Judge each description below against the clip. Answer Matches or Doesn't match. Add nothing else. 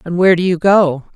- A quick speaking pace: Matches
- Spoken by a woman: Matches